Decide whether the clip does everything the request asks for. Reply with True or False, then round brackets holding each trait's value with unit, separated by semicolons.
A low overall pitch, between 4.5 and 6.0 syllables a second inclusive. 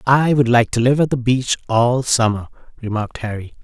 True (120 Hz; 5.3 syllables/s)